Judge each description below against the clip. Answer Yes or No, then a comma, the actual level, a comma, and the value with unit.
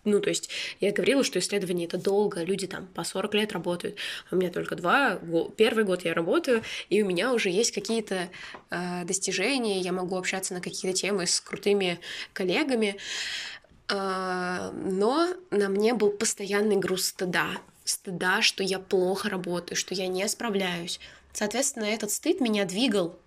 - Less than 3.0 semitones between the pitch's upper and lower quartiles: Yes, narrow, 2.4 semitones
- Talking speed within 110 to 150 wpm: No, fast, 160 wpm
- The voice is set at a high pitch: Yes, high, 195 Hz